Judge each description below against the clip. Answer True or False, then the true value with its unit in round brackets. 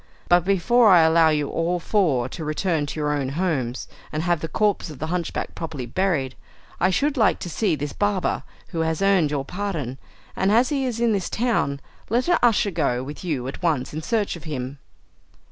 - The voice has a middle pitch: True (165 Hz)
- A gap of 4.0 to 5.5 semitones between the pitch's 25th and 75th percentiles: True (5.2 semitones)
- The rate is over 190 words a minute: True (205 wpm)